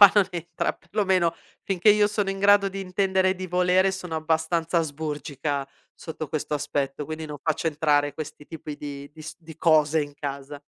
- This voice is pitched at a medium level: Yes, medium, 160 Hz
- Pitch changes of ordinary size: Yes, average, 4.0 semitones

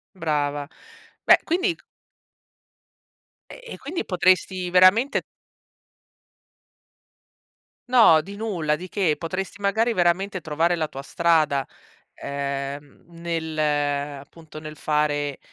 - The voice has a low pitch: No, medium, 170 Hz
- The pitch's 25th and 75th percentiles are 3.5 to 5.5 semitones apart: Yes, average, 4.2 semitones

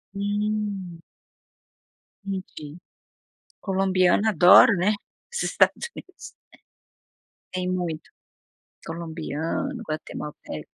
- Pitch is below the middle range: No, medium, 185 Hz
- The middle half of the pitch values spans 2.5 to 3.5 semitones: No, average, 3.9 semitones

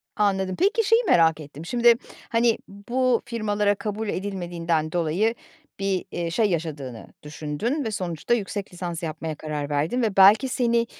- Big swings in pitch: Yes, wide, 5.9 semitones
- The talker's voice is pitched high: Yes, high, 195 Hz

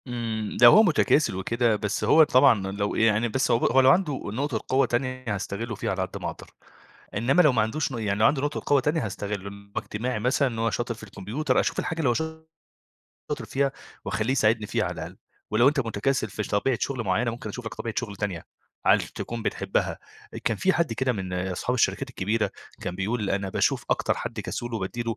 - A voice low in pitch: Yes, low, 115 Hz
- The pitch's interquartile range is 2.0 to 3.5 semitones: No, average, 4.1 semitones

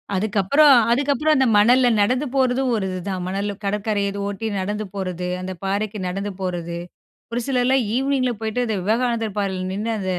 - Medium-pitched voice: No, high, 210 Hz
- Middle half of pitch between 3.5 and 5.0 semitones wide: Yes, average, 4.5 semitones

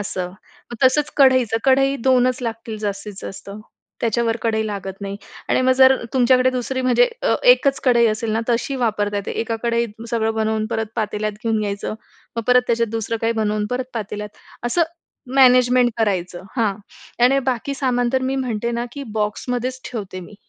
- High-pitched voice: Yes, high, 230 Hz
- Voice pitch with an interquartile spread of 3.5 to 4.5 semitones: No, average, 3.0 semitones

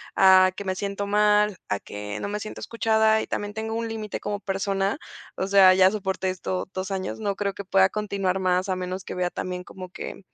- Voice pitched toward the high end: Yes, high, 195 Hz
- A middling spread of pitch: No, narrow, 1.9 semitones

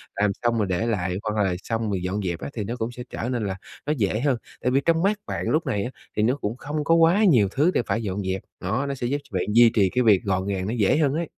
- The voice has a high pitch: No, low, 115 Hz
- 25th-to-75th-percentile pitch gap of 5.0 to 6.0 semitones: Yes, wide, 5.6 semitones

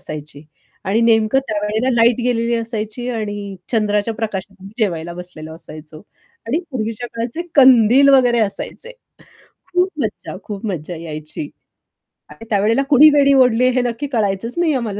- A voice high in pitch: Yes, high, 225 Hz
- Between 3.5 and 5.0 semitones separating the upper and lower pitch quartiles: Yes, average, 4.1 semitones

